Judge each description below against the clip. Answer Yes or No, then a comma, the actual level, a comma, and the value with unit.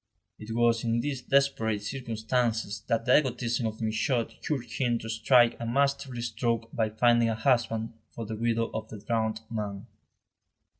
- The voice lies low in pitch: Yes, low, 115 Hz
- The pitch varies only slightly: Yes, narrow, 1.6 semitones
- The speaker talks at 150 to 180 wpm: Yes, average, 160 wpm